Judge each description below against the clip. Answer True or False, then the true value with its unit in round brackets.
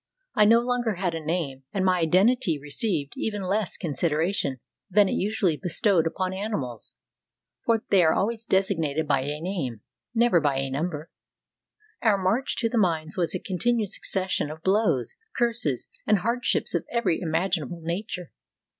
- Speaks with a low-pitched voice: False (180 Hz)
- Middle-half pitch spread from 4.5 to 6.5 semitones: True (5.0 semitones)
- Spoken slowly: False (155 wpm)